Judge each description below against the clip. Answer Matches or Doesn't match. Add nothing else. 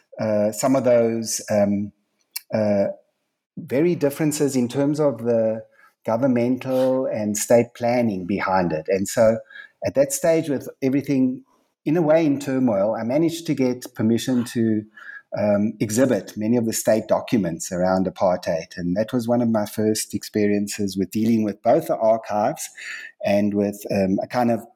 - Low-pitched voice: Matches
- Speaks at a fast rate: Doesn't match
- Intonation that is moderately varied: Matches